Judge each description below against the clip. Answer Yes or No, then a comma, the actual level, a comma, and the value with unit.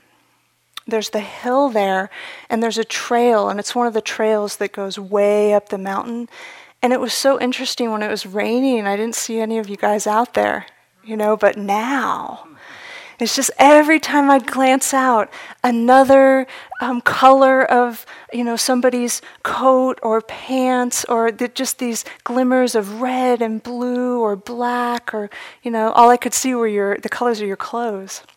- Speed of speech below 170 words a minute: No, average, 180 wpm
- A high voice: Yes, high, 240 Hz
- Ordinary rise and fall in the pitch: Yes, average, 3.1 semitones